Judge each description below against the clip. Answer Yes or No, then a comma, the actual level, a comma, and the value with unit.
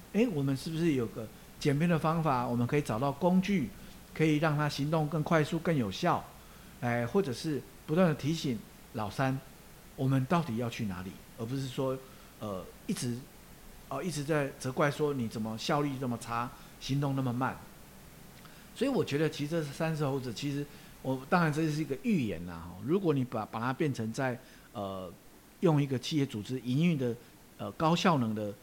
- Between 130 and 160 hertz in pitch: Yes, medium, 140 Hz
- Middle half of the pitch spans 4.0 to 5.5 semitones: Yes, average, 4.8 semitones